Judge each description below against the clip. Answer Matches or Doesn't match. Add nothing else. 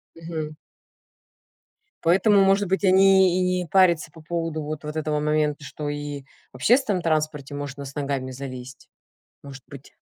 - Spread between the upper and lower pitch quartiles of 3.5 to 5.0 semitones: Matches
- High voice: Doesn't match